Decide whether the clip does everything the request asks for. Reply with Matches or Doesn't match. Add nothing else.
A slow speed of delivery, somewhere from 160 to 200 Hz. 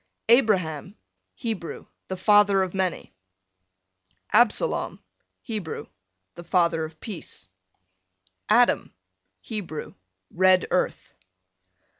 Matches